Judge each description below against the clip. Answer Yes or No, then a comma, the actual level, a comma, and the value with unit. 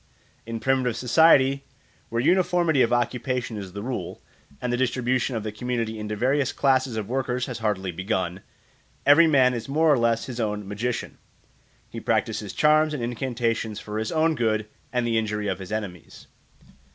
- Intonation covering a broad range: No, average, 3.5 semitones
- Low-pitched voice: Yes, low, 120 Hz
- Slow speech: No, average, 170 wpm